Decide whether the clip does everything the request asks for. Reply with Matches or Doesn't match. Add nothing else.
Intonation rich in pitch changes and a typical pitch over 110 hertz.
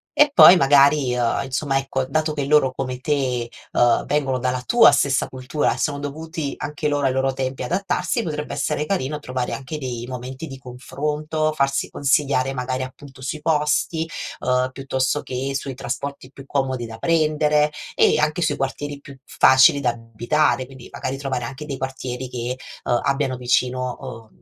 Doesn't match